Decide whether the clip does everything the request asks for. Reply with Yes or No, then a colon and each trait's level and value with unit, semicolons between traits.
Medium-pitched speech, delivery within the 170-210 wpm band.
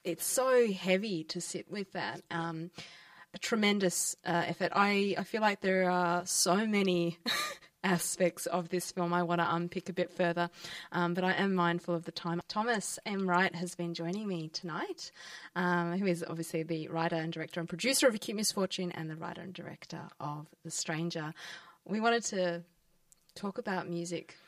Yes: medium, 175 Hz; average, 180 wpm